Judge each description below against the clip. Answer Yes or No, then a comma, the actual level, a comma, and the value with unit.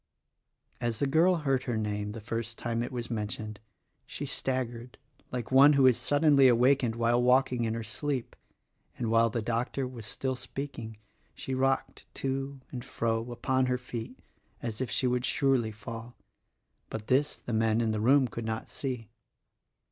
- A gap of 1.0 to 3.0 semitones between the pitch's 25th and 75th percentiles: Yes, average, 2.7 semitones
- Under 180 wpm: Yes, average, 170 wpm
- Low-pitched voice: Yes, low, 120 Hz